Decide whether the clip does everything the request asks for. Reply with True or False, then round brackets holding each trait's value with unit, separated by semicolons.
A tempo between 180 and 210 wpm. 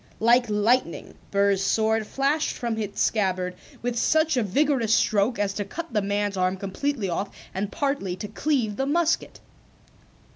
False (155 wpm)